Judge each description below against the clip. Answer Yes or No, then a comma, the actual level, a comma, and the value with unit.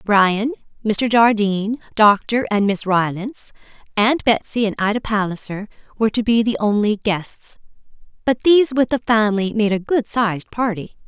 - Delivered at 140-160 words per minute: Yes, average, 150 wpm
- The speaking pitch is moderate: No, high, 215 Hz